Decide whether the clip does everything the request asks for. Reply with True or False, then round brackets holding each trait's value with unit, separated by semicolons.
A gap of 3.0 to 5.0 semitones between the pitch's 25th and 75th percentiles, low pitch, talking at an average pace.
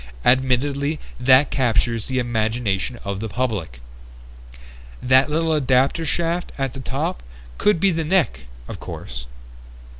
False (4.7 semitones; 130 Hz; 125 wpm)